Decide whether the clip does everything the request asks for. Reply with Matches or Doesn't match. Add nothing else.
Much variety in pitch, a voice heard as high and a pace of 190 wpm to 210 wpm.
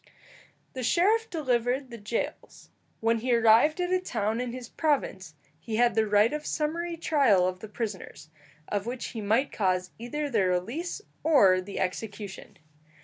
Doesn't match